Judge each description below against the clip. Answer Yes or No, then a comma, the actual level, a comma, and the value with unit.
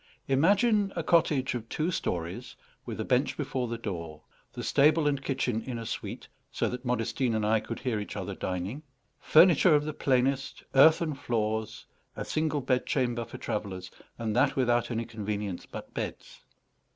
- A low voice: Yes, low, 125 Hz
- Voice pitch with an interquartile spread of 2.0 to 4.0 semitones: No, average, 4.8 semitones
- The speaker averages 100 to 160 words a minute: No, average, 170 wpm